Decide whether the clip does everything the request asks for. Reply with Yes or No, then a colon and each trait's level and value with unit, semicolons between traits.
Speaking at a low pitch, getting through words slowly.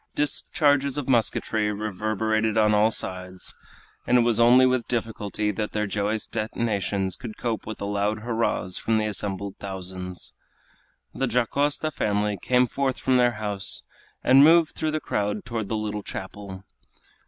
No: low, 110 Hz; average, 155 wpm